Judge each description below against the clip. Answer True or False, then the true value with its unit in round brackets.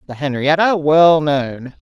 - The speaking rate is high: False (130 wpm)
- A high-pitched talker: False (150 Hz)